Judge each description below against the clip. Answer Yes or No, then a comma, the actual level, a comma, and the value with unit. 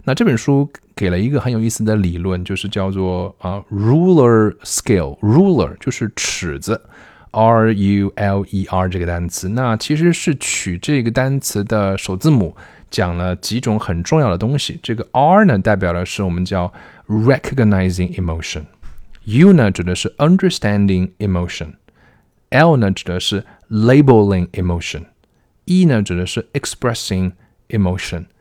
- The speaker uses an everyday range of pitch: Yes, average, 4.9 semitones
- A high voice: No, low, 100 Hz